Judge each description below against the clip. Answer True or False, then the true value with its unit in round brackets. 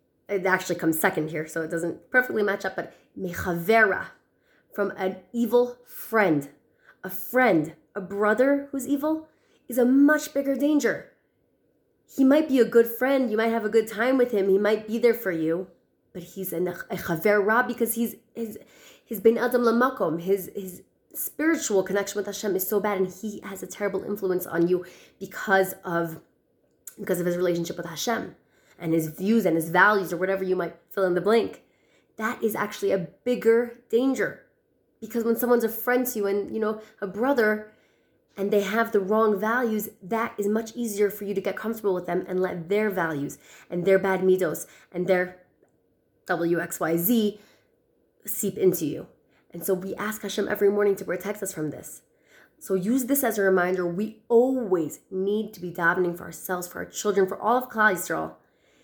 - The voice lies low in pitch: False (205 Hz)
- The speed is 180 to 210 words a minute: True (185 wpm)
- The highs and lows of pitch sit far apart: False (3.9 semitones)